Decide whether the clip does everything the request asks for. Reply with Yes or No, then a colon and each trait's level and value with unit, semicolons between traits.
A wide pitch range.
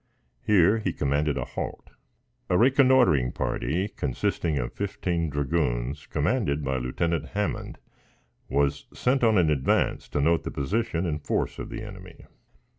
Yes: wide, 6.4 semitones